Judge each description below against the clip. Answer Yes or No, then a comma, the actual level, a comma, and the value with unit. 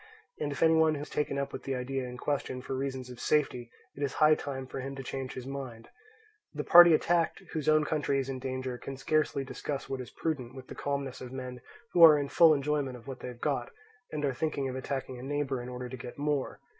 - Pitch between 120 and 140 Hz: Yes, low, 135 Hz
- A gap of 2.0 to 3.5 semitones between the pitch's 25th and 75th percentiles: Yes, narrow, 2.5 semitones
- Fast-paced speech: Yes, fast, 245 wpm